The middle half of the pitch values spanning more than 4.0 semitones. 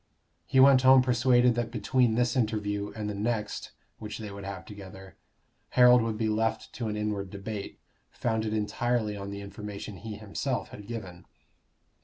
No: average, 2.8 semitones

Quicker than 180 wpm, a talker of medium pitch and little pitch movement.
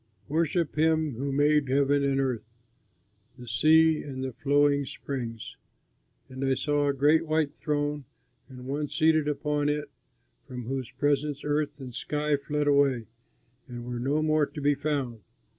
No: average, 155 wpm; medium, 145 Hz; narrow, 2.1 semitones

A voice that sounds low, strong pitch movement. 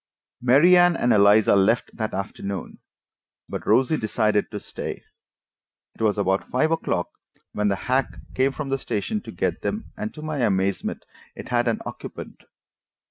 Yes: low, 120 Hz; wide, 6.1 semitones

